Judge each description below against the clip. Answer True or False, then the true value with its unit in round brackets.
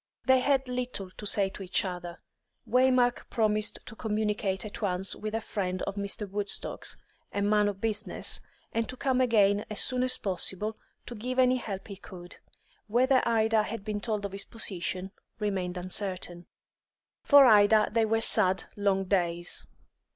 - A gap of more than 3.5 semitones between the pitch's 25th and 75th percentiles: False (2.9 semitones)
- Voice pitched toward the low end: False (210 Hz)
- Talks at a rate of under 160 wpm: False (165 wpm)